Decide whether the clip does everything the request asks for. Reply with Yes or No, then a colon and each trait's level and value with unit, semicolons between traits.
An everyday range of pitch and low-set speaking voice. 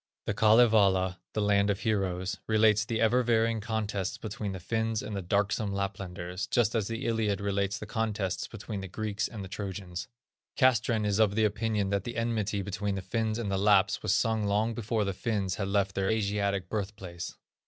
No: narrow, 2.2 semitones; low, 105 Hz